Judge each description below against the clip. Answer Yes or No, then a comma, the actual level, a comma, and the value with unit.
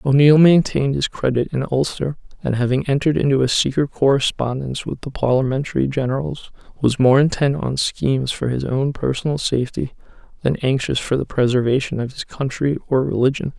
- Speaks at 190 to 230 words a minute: No, average, 165 wpm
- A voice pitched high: No, low, 135 Hz